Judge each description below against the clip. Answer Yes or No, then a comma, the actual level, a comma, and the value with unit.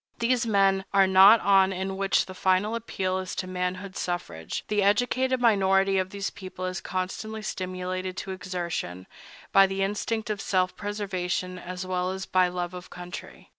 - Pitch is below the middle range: No, high, 190 Hz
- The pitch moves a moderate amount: No, narrow, 1.6 semitones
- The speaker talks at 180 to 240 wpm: No, average, 170 wpm